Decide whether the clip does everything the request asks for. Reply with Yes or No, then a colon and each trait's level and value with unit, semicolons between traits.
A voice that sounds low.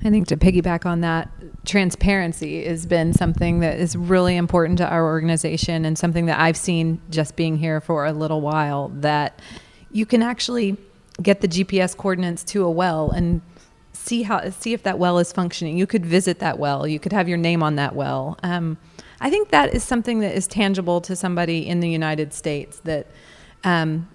No: medium, 170 Hz